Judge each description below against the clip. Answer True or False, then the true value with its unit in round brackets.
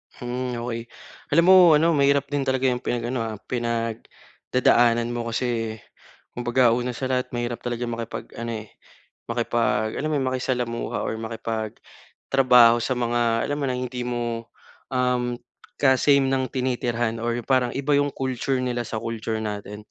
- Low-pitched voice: True (120 Hz)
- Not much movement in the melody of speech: True (1.8 semitones)